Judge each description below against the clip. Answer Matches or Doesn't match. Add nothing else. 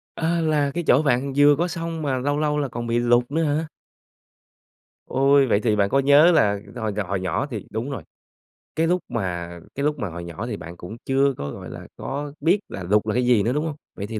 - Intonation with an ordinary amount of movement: Doesn't match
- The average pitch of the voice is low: Matches